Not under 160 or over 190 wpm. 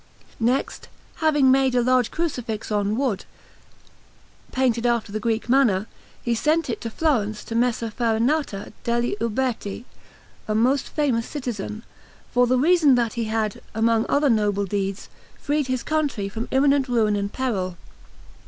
No: average, 145 wpm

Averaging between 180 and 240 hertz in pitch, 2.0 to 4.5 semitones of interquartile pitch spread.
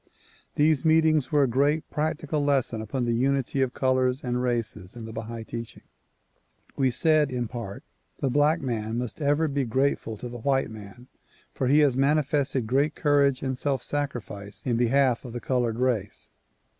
No: low, 130 Hz; average, 3.3 semitones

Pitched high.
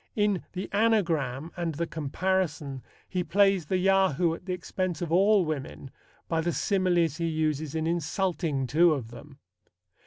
No: medium, 170 Hz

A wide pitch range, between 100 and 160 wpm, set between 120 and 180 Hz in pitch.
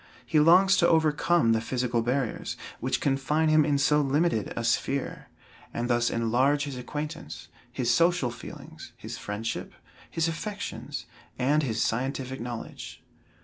No: average, 4.4 semitones; average, 140 wpm; low, 135 Hz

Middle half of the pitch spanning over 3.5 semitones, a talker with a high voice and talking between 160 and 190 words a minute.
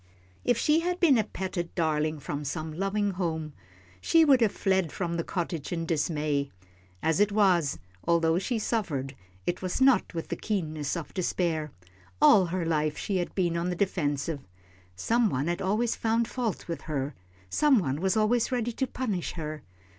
No: wide, 5.4 semitones; medium, 175 Hz; average, 175 wpm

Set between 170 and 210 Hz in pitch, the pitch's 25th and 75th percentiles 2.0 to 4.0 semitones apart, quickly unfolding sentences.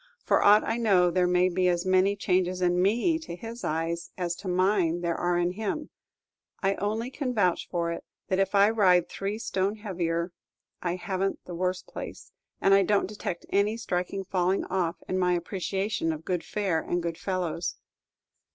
No: medium, 185 Hz; narrow, 2.4 semitones; average, 190 wpm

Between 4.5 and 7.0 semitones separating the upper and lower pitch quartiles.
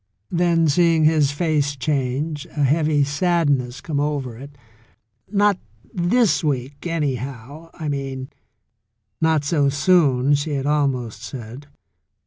No: average, 3.0 semitones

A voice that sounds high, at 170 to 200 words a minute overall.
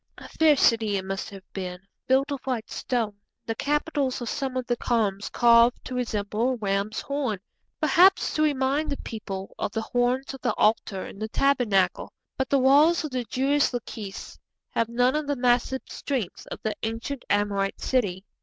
Yes: high, 245 Hz; average, 180 wpm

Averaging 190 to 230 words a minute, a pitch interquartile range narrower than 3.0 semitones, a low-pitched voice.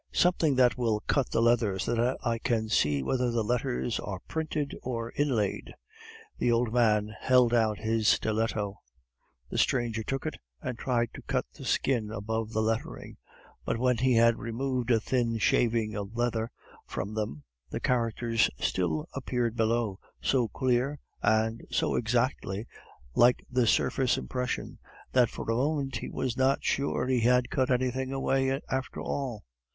No: average, 160 wpm; narrow, 2.5 semitones; low, 120 Hz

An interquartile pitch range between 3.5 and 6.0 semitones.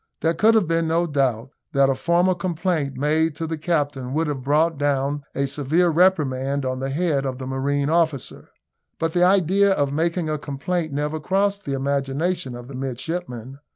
Yes: average, 3.9 semitones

